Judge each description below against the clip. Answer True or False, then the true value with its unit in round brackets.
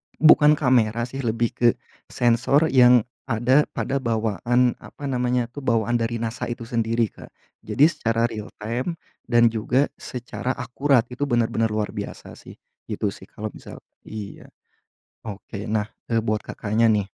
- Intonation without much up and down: True (2.1 semitones)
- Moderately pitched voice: False (120 Hz)